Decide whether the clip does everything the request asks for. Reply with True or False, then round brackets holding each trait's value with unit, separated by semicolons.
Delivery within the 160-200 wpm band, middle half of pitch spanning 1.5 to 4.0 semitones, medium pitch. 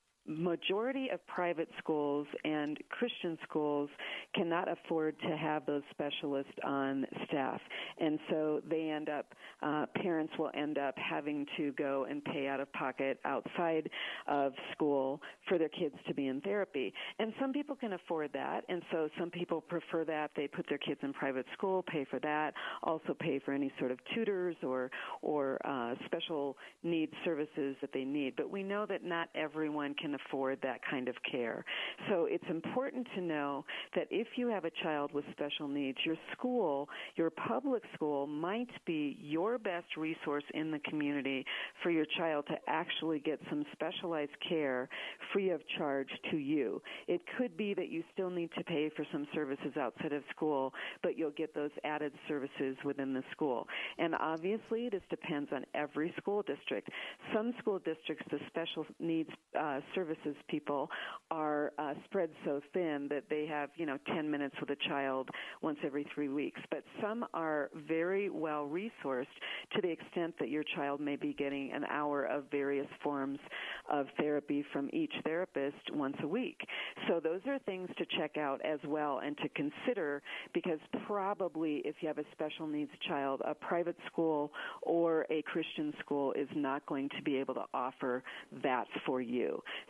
True (175 wpm; 3.2 semitones; 155 Hz)